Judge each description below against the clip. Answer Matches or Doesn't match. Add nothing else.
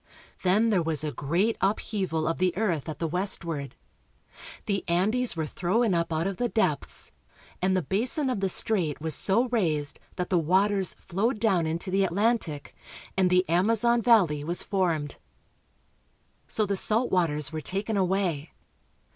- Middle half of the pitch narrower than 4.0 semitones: Doesn't match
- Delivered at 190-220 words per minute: Doesn't match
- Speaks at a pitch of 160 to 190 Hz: Matches